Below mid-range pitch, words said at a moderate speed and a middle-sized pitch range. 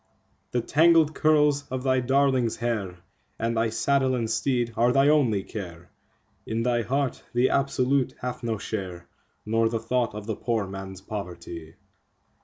Yes: low, 120 Hz; average, 150 wpm; average, 3.8 semitones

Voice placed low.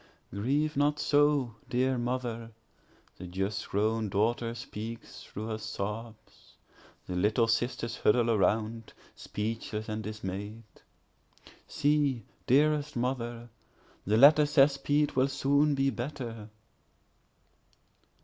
Yes: low, 115 Hz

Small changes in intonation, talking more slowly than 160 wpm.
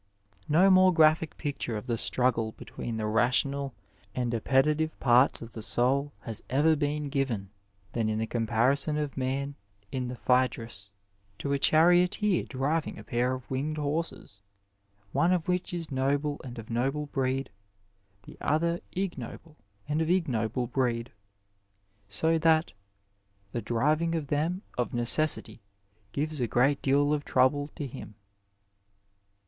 No: average, 4.4 semitones; average, 145 wpm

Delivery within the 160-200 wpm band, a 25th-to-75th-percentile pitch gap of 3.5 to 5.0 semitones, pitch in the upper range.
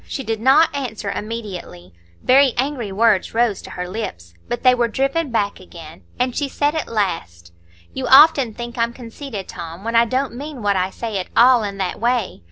Yes: average, 195 wpm; average, 4.7 semitones; high, 230 Hz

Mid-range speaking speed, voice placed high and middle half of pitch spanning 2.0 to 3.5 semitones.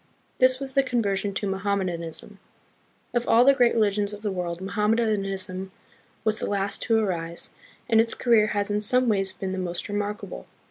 Yes: average, 180 wpm; high, 205 Hz; average, 2.8 semitones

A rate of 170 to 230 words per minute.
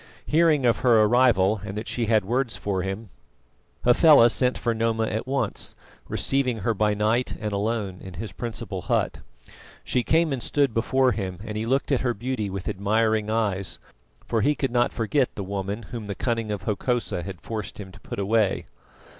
Yes: average, 190 wpm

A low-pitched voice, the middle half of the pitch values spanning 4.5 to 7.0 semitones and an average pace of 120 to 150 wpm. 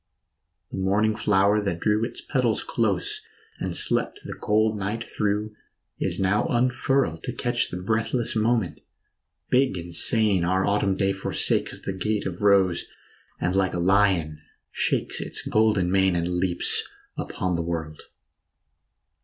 No: low, 100 Hz; average, 3.3 semitones; average, 145 wpm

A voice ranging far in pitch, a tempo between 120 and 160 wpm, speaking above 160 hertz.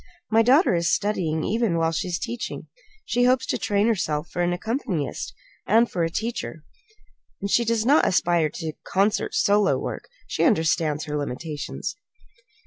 Yes: wide, 5.9 semitones; average, 155 wpm; high, 190 Hz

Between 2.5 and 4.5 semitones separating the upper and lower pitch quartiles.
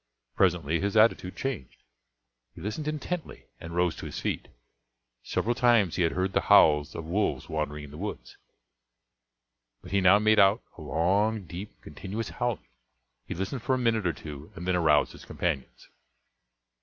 No: average, 5.0 semitones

